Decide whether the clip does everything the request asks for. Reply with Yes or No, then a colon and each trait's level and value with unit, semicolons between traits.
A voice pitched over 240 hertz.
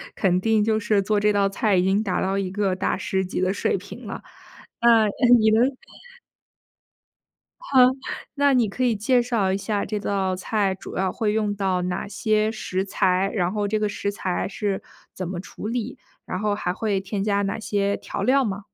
No: high, 205 Hz